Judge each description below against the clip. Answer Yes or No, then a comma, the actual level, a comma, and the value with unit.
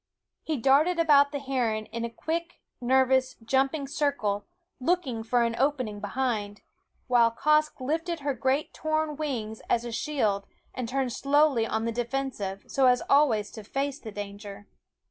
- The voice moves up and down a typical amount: Yes, average, 4.1 semitones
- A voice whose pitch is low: No, very high, 260 Hz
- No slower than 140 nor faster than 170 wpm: Yes, average, 155 wpm